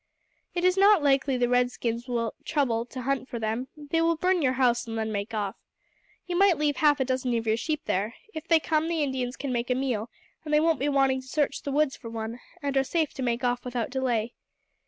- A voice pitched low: No, very high, 260 Hz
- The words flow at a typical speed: No, fast, 240 wpm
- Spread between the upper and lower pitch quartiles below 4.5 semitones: Yes, average, 4.0 semitones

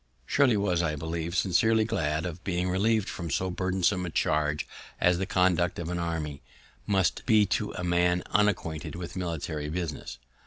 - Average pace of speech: Yes, average, 165 wpm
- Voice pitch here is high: No, very low, 90 Hz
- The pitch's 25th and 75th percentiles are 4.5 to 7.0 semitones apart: No, average, 2.7 semitones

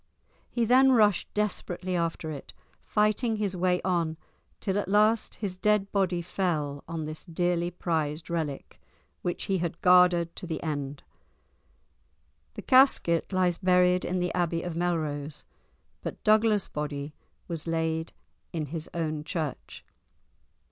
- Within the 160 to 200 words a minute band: No, slow, 135 wpm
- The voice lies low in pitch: No, medium, 175 Hz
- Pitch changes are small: No, average, 3.3 semitones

